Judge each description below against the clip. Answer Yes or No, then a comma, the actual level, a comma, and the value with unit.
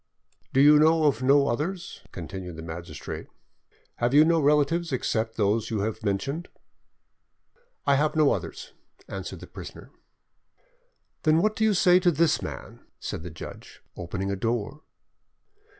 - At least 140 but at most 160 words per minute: Yes, average, 150 wpm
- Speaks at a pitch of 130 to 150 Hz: Yes, medium, 140 Hz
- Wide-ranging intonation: Yes, wide, 7.5 semitones